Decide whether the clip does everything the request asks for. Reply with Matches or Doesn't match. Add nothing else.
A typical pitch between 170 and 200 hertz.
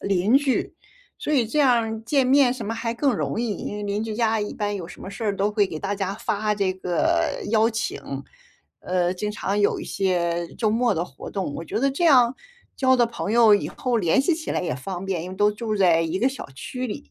Doesn't match